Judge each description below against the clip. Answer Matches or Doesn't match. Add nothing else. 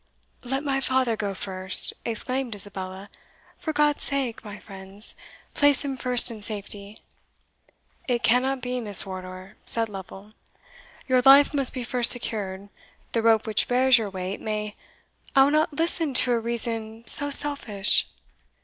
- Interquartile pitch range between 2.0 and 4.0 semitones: Doesn't match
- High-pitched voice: Matches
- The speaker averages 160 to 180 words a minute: Doesn't match